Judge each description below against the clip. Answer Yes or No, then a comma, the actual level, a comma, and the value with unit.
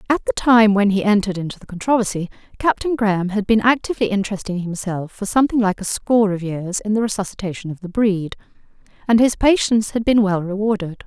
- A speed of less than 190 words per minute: No, average, 195 wpm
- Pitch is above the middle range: Yes, high, 205 Hz